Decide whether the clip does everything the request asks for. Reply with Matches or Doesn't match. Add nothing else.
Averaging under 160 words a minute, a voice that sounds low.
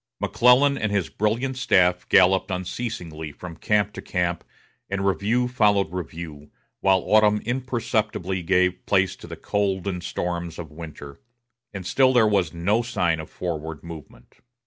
Matches